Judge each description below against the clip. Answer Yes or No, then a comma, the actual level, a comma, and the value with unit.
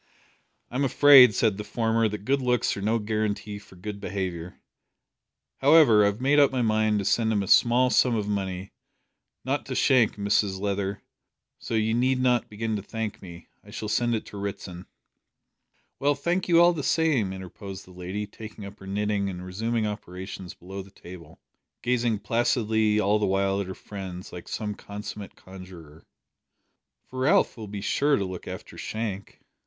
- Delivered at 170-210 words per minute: Yes, average, 180 wpm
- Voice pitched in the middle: No, low, 105 Hz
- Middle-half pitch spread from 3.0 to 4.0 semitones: Yes, average, 3.3 semitones